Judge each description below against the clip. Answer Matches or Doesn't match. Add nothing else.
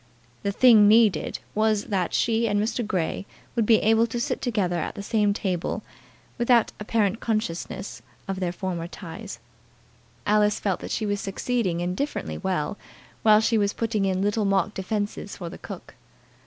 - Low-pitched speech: Doesn't match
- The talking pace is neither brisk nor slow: Matches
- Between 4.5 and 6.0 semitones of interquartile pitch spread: Doesn't match